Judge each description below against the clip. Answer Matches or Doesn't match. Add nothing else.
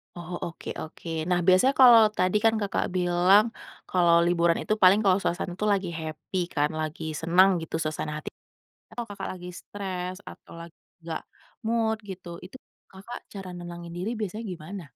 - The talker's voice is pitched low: Doesn't match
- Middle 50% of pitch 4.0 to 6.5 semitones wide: Doesn't match